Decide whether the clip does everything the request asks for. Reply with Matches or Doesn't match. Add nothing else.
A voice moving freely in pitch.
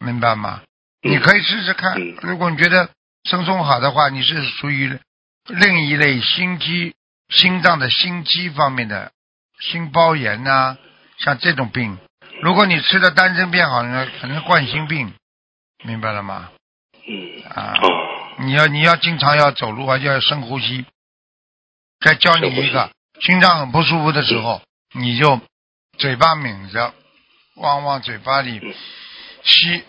Matches